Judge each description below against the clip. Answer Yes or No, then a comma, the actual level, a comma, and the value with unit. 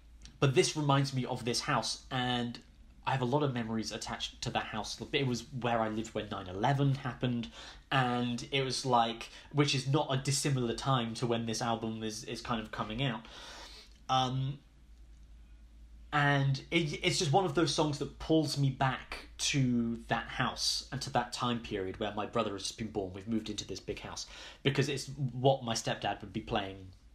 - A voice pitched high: No, low, 120 Hz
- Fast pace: No, average, 195 wpm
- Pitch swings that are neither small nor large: Yes, average, 3.7 semitones